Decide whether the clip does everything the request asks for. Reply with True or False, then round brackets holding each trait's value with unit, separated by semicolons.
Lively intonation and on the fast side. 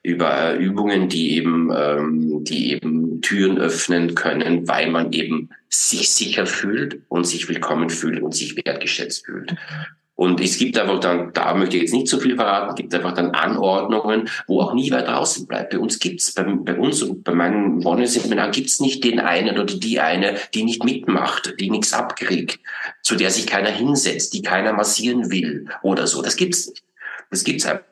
True (5.9 semitones; 200 wpm)